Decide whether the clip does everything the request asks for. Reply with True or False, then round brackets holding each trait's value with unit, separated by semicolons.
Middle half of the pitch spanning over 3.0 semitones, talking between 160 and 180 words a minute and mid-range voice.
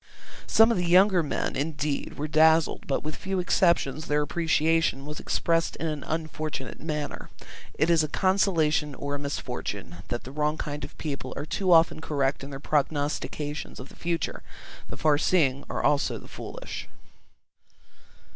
False (2.5 semitones; 165 wpm; 150 Hz)